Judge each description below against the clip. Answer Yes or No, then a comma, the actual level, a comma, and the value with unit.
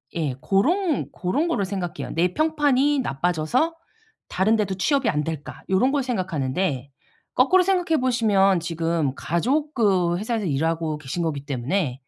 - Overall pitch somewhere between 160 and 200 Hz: Yes, high, 190 Hz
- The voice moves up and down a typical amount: No, wide, 8.3 semitones